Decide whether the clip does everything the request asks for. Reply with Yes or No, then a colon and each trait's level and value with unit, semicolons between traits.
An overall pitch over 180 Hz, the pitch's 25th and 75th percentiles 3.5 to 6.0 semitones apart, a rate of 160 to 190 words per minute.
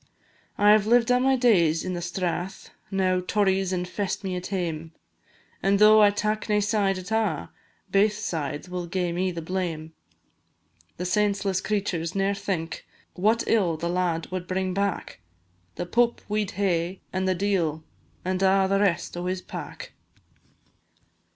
No: high, 190 Hz; narrow, 2.6 semitones; average, 165 wpm